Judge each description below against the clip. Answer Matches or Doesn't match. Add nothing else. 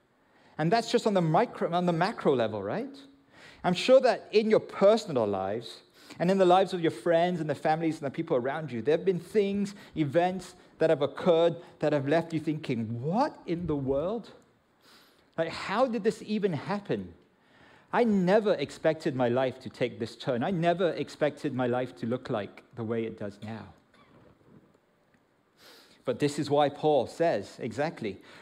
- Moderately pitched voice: Matches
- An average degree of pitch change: Doesn't match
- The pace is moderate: Matches